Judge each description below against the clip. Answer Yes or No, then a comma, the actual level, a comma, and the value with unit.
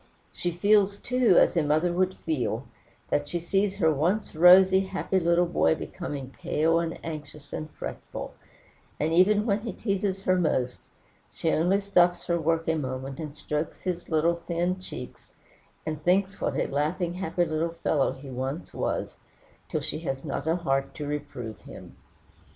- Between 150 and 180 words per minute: Yes, average, 170 wpm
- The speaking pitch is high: No, medium, 165 Hz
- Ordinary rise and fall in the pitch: Yes, average, 3.7 semitones